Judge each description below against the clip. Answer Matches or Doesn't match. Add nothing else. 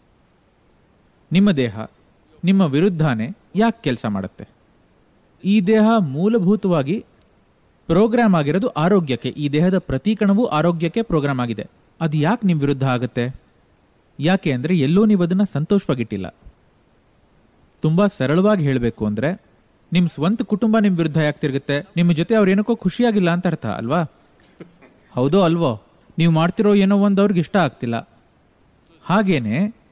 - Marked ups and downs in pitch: Matches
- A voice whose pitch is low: Doesn't match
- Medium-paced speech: Doesn't match